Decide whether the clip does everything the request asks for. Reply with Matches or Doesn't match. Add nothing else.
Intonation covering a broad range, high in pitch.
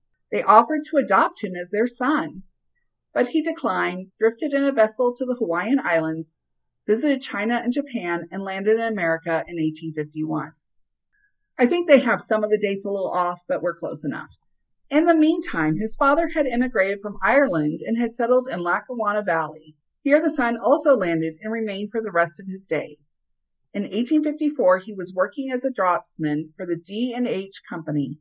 Matches